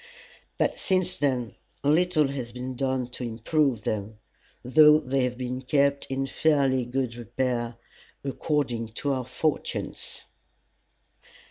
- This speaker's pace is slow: Yes, slow, 120 wpm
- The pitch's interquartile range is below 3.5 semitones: Yes, average, 2.8 semitones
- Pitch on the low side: Yes, low, 130 Hz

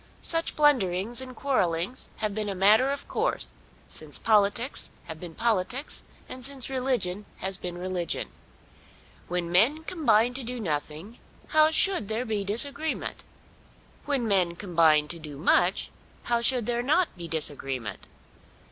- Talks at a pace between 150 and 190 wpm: No, average, 140 wpm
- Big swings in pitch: Yes, wide, 6.6 semitones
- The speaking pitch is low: No, high, 215 Hz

